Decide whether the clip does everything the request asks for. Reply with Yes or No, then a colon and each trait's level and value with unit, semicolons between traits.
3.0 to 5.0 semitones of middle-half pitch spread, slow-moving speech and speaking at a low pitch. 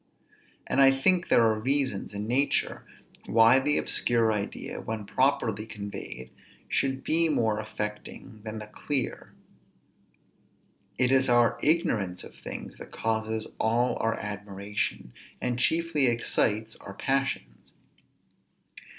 Yes: average, 4.1 semitones; slow, 120 wpm; low, 115 Hz